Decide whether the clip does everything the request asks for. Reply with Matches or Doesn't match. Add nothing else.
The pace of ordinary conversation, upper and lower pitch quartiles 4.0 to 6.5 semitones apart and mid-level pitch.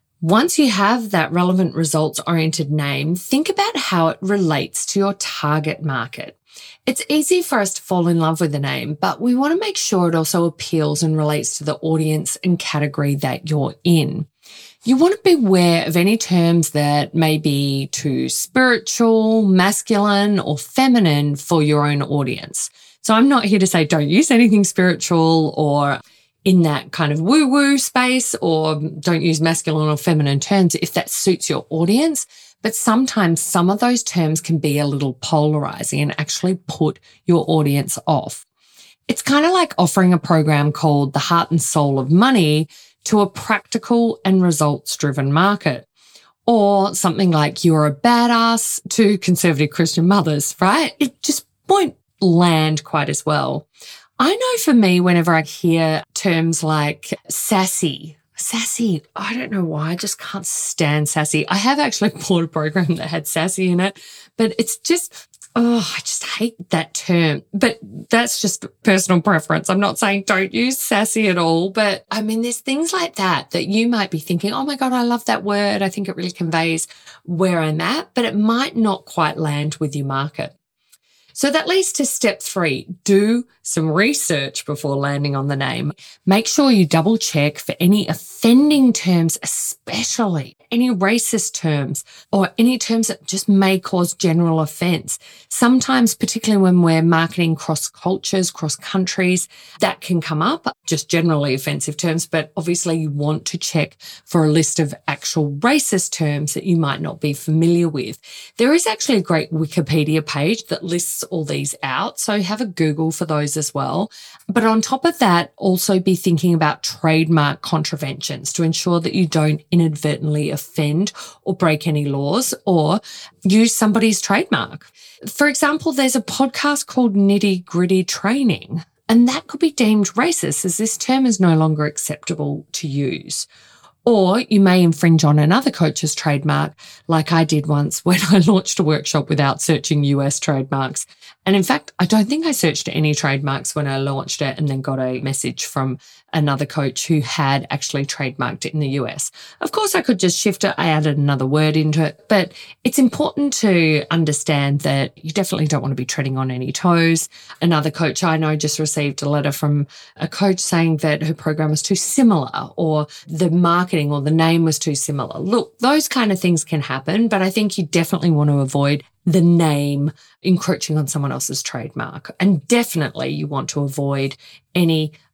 Matches